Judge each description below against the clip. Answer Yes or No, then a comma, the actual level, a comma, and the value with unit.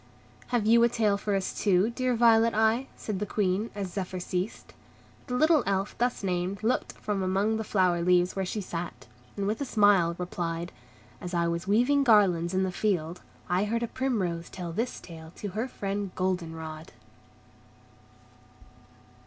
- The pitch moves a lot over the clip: No, average, 3.7 semitones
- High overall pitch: Yes, high, 195 Hz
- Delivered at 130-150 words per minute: No, average, 170 wpm